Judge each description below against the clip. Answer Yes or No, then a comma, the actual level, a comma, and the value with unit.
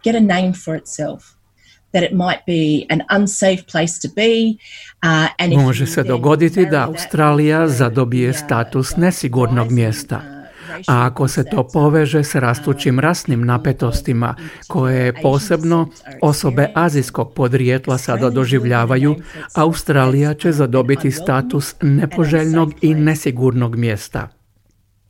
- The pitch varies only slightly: No, average, 4.1 semitones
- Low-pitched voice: No, medium, 145 Hz